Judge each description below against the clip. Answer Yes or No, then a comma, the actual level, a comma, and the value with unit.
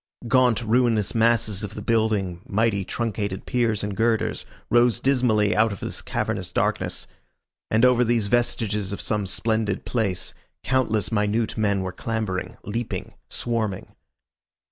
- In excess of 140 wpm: No, slow, 135 wpm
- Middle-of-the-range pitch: No, low, 110 Hz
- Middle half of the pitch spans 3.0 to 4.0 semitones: No, narrow, 2.4 semitones